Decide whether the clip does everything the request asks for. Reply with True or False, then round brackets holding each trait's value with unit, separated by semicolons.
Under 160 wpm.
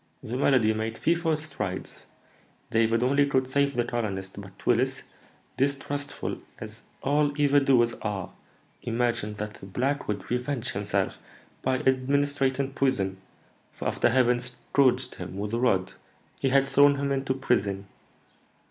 True (140 wpm)